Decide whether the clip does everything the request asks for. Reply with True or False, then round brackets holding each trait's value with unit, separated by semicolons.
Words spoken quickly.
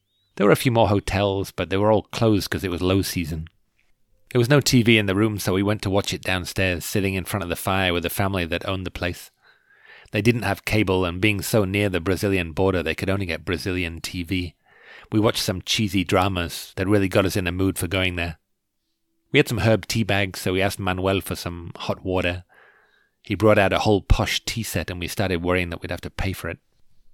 True (240 wpm)